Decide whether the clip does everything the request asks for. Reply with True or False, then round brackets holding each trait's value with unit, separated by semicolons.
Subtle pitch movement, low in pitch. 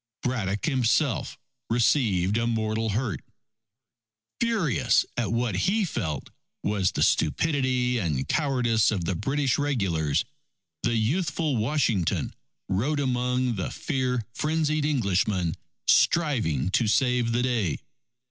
False (5.5 semitones; 120 Hz)